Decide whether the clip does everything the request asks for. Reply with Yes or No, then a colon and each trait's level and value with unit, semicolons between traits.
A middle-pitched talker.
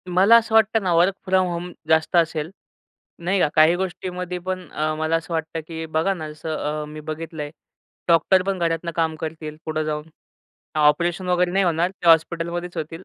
Yes: medium, 165 Hz